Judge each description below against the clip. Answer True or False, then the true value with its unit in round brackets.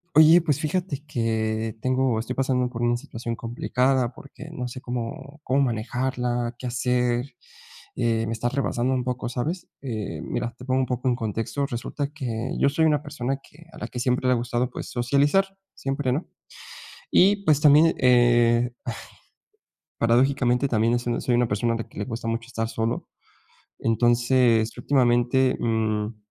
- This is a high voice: False (125 Hz)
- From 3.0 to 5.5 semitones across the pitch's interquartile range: False (2.6 semitones)